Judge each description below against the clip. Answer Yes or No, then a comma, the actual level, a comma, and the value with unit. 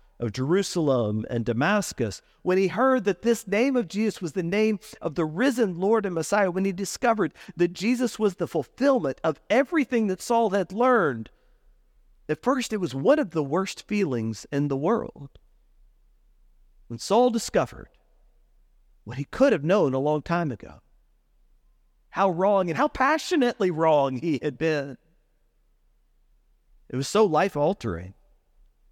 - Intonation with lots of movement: Yes, wide, 7.9 semitones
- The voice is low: No, medium, 185 Hz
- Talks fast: No, average, 150 wpm